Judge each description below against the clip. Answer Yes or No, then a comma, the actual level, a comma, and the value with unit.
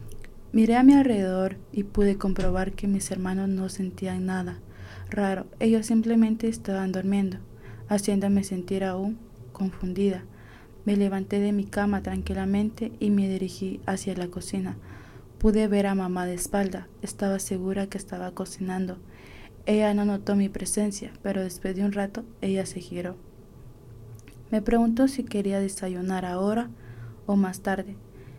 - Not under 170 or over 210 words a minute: No, average, 140 wpm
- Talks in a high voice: Yes, high, 195 Hz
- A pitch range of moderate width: No, narrow, 1.9 semitones